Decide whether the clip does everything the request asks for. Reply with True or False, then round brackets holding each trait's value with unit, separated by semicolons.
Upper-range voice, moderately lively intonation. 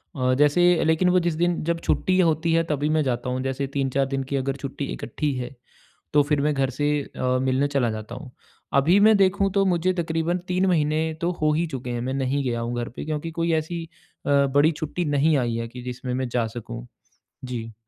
False (145 Hz; 4.5 semitones)